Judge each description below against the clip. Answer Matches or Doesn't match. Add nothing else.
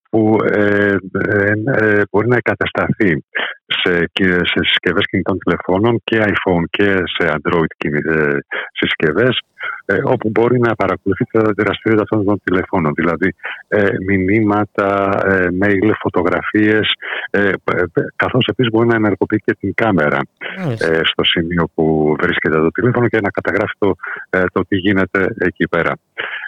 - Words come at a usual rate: Matches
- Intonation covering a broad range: Doesn't match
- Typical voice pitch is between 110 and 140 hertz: Doesn't match